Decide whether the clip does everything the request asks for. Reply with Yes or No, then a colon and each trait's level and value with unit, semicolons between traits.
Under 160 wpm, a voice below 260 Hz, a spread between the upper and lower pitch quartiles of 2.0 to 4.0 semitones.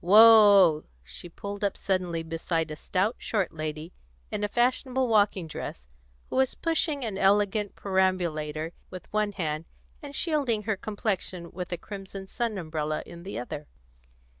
No: average, 150 wpm; high, 190 Hz; average, 4.4 semitones